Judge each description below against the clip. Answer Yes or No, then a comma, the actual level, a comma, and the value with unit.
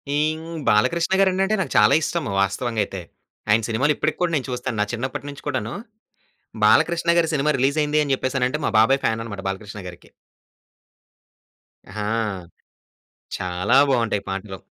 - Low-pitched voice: Yes, low, 130 Hz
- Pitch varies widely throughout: Yes, wide, 6.3 semitones